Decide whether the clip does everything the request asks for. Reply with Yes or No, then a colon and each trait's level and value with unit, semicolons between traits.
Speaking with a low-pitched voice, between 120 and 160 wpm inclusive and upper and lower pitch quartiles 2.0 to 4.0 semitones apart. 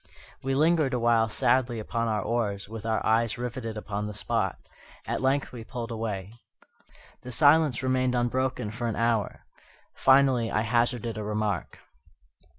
Yes: low, 115 Hz; average, 150 wpm; average, 2.7 semitones